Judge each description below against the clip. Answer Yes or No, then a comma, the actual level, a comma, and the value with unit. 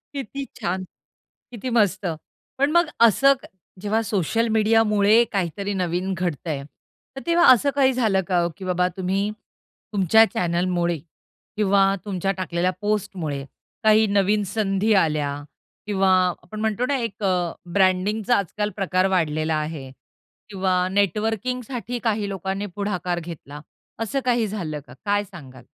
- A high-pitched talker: Yes, high, 200 Hz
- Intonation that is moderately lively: Yes, average, 3.4 semitones